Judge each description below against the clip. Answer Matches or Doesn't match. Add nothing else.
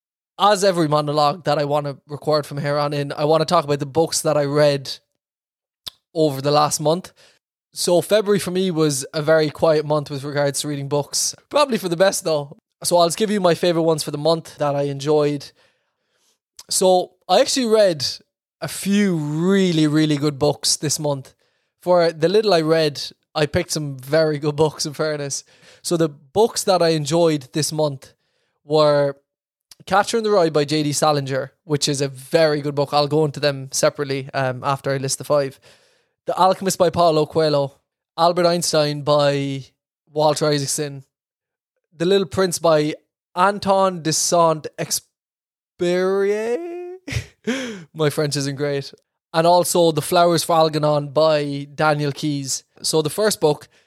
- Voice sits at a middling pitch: Matches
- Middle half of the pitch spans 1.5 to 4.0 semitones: Matches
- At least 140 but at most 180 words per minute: Matches